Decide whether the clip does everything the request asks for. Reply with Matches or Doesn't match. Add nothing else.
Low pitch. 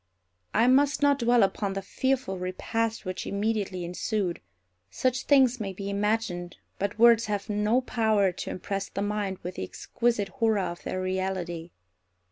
Doesn't match